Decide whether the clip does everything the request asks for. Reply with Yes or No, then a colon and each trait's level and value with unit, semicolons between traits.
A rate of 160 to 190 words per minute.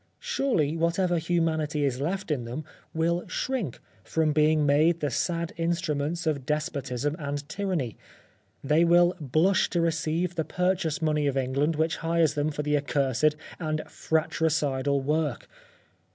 No: average, 150 wpm